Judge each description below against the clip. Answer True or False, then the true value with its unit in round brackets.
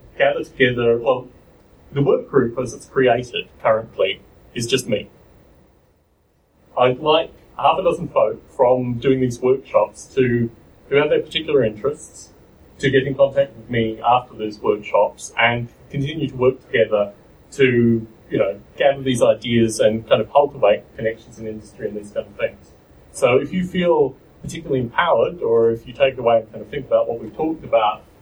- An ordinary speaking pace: True (175 wpm)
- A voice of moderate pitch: False (125 Hz)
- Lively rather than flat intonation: False (3.2 semitones)